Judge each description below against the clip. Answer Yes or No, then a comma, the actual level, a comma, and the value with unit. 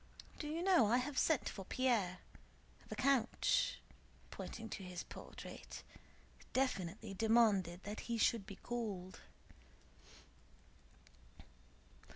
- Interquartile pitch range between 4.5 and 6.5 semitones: Yes, average, 4.8 semitones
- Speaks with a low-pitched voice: No, high, 225 Hz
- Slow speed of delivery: Yes, slow, 105 wpm